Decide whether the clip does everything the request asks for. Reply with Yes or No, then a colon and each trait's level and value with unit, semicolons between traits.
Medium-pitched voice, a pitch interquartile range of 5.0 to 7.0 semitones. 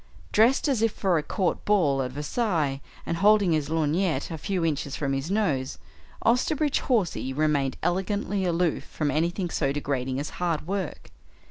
Yes: medium, 165 Hz; wide, 5.6 semitones